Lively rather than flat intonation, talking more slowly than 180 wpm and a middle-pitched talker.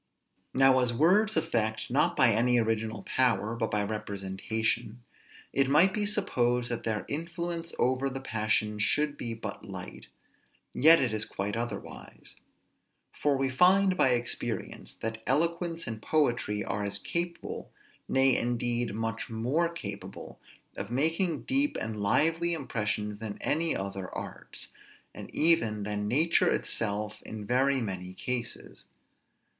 No: wide, 6.4 semitones; slow, 135 wpm; low, 120 Hz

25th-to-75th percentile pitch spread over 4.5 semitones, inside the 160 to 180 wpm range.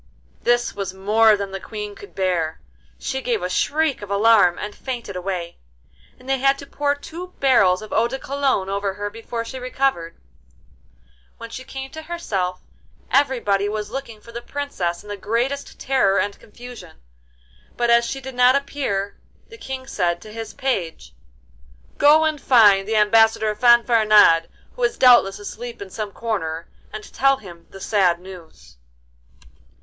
Yes: average, 5.2 semitones; average, 165 wpm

